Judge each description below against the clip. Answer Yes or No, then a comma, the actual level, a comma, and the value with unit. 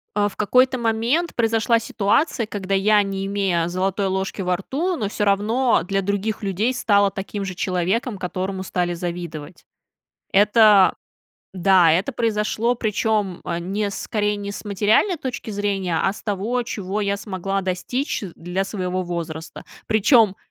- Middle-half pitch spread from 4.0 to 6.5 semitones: No, average, 2.8 semitones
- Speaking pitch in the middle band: No, high, 200 Hz